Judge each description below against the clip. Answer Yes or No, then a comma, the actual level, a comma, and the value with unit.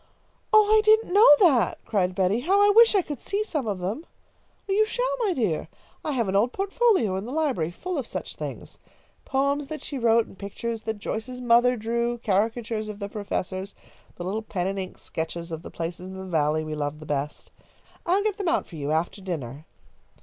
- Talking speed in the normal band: No, fast, 210 wpm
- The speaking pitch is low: No, high, 225 Hz